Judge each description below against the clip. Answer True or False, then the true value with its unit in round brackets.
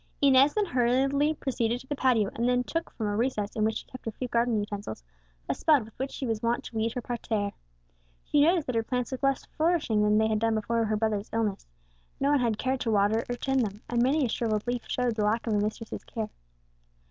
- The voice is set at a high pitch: True (235 Hz)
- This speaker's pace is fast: True (240 wpm)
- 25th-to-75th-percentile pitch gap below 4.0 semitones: True (3.3 semitones)